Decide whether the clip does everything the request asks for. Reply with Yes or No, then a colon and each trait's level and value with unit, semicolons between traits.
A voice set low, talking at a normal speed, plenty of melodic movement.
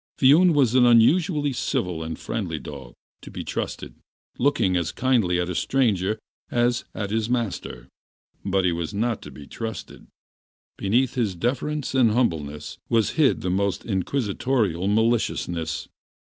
No: low, 110 Hz; slow, 130 wpm; wide, 6.0 semitones